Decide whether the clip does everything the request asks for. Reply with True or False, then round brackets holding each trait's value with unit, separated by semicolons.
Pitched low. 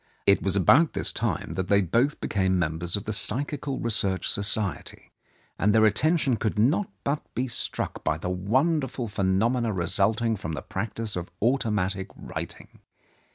True (105 Hz)